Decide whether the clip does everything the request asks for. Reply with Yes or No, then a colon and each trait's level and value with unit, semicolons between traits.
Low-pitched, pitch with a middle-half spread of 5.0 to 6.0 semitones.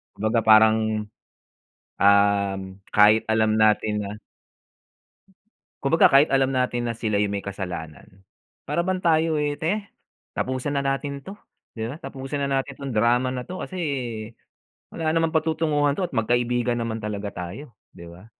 Yes: low, 120 Hz; average, 5.3 semitones